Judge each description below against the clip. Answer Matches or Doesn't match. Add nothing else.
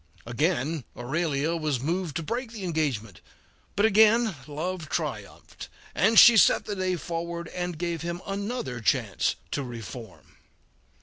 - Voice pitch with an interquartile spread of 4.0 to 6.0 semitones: Matches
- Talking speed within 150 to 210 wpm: Doesn't match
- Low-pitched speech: Doesn't match